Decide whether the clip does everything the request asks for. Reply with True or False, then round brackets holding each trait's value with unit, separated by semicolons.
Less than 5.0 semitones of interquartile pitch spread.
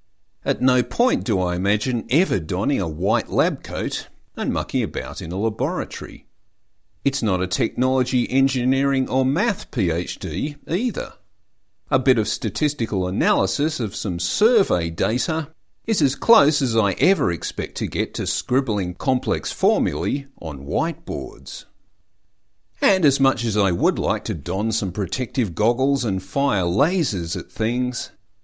False (5.4 semitones)